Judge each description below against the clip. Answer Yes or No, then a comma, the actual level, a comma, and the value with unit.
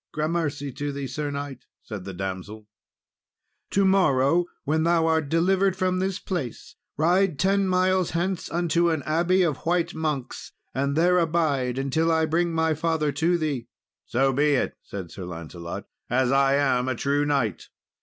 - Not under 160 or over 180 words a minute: Yes, average, 165 wpm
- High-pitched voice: No, medium, 155 Hz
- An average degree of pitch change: Yes, average, 4.2 semitones